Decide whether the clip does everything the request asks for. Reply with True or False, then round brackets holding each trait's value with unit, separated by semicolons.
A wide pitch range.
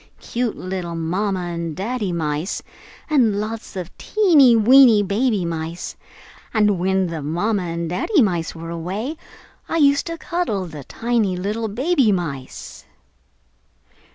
True (5.7 semitones)